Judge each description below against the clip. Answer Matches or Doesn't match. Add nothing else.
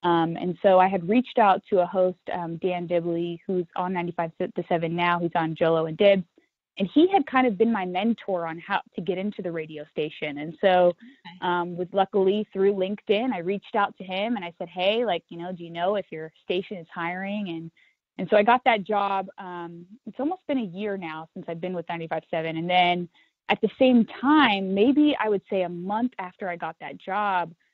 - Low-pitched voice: Doesn't match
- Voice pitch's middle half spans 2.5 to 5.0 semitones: Matches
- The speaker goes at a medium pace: Doesn't match